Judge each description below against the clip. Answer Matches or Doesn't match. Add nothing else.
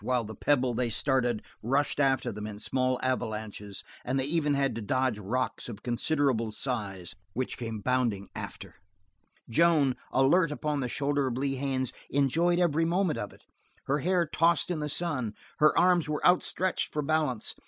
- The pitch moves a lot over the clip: Doesn't match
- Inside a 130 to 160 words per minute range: Doesn't match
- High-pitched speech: Doesn't match